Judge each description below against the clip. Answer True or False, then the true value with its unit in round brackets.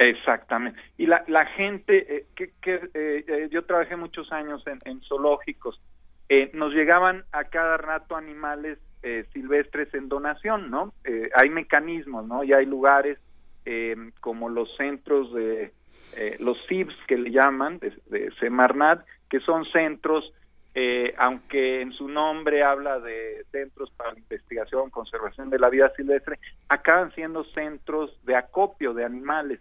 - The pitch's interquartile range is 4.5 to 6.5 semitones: False (3.7 semitones)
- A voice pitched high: False (150 Hz)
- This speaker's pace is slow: False (155 wpm)